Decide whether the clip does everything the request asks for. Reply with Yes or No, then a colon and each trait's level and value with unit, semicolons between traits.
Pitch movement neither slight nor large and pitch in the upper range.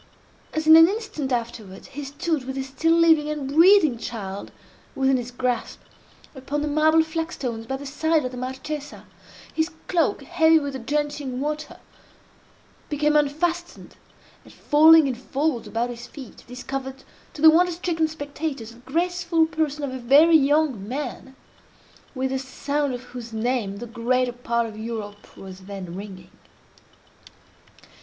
Yes: average, 4.3 semitones; very high, 275 Hz